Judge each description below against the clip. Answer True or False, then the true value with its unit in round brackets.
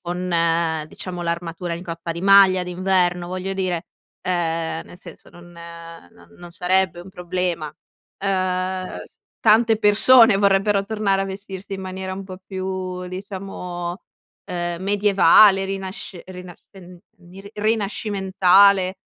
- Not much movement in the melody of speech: True (1.9 semitones)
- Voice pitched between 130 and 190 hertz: True (185 Hz)